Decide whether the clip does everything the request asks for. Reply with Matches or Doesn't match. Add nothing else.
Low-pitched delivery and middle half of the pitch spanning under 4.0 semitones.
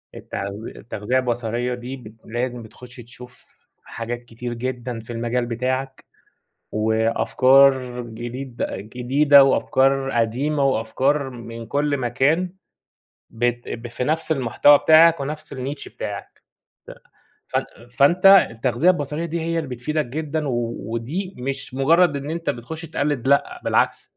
Matches